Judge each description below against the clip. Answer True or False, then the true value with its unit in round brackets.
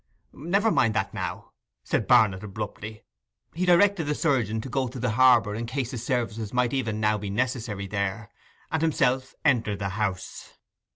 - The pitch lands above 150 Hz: False (115 Hz)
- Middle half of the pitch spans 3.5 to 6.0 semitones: True (3.9 semitones)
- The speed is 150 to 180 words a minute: True (170 wpm)